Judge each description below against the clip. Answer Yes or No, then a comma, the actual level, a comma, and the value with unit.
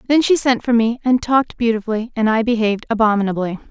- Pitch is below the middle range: No, high, 230 Hz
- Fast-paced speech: No, average, 195 wpm